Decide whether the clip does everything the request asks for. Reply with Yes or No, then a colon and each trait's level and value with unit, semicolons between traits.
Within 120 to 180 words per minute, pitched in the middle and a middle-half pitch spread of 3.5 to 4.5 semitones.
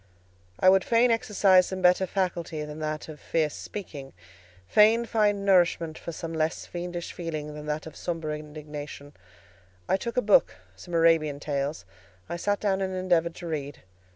Yes: average, 160 wpm; medium, 165 Hz; average, 3.9 semitones